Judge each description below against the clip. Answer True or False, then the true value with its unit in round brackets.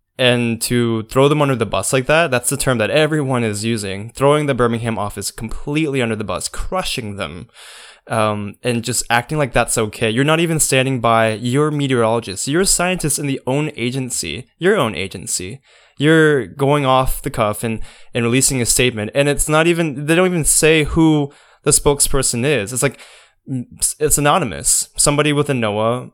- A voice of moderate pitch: False (130 Hz)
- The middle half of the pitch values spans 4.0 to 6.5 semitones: True (4.4 semitones)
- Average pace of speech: True (180 wpm)